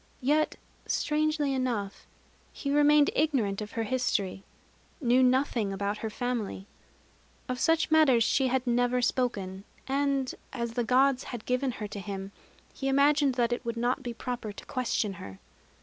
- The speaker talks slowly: No, average, 155 wpm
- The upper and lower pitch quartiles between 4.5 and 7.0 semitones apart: No, average, 3.7 semitones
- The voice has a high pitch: Yes, very high, 250 Hz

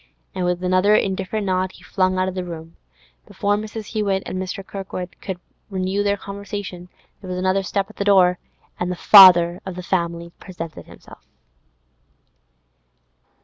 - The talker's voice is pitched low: No, medium, 185 Hz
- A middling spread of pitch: No, narrow, 1.8 semitones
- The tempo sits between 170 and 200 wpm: No, average, 155 wpm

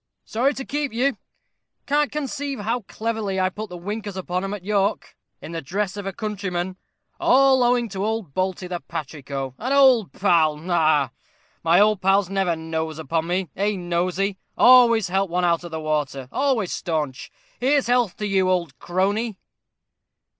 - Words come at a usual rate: Yes, average, 170 wpm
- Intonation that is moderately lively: Yes, average, 4.6 semitones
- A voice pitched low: No, high, 190 Hz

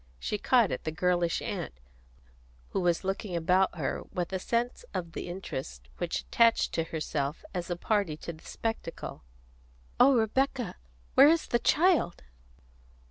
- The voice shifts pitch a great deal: Yes, wide, 5.7 semitones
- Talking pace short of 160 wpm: Yes, average, 150 wpm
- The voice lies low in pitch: No, medium, 180 Hz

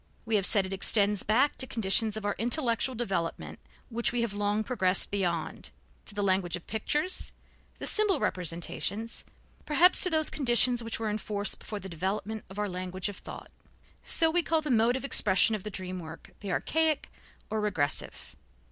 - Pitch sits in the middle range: No, high, 215 Hz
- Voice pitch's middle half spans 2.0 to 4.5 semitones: Yes, average, 4.1 semitones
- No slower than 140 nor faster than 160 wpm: No, average, 185 wpm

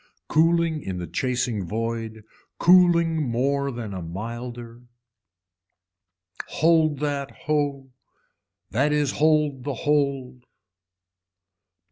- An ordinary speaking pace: No, slow, 85 wpm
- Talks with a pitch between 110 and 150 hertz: Yes, medium, 140 Hz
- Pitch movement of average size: Yes, average, 4.3 semitones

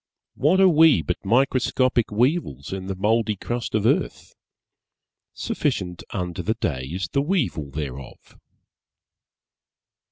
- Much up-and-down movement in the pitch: Yes, wide, 6.8 semitones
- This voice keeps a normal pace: No, slow, 120 wpm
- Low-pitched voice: Yes, low, 105 Hz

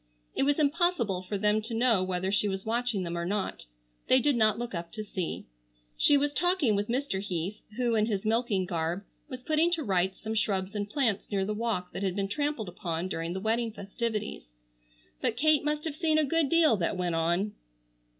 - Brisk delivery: Yes, fast, 210 wpm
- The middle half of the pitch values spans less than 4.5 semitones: No, average, 5.3 semitones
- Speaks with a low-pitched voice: No, high, 215 Hz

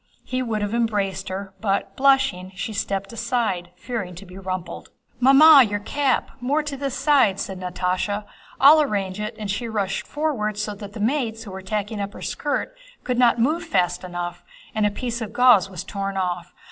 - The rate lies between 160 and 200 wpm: Yes, average, 190 wpm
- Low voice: No, high, 210 Hz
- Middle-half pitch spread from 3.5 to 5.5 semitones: Yes, average, 4.6 semitones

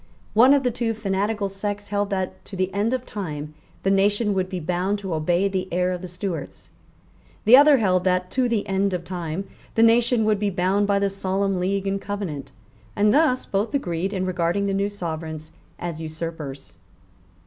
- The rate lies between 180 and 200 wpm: Yes, average, 190 wpm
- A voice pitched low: No, high, 195 Hz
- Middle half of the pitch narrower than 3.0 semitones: Yes, narrow, 2.5 semitones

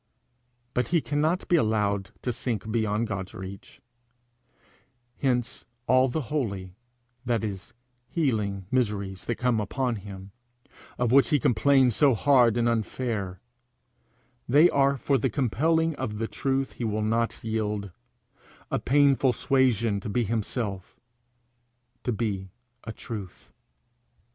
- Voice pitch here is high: No, low, 115 Hz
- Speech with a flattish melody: No, average, 4.2 semitones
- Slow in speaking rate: Yes, slow, 130 wpm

